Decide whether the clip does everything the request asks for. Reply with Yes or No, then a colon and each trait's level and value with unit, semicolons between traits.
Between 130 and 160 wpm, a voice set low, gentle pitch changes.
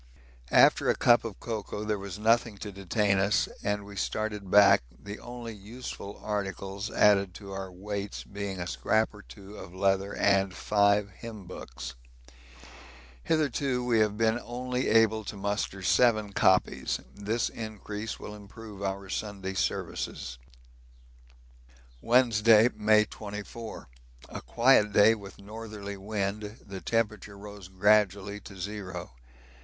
Yes: slow, 135 wpm; low, 105 Hz; narrow, 1.8 semitones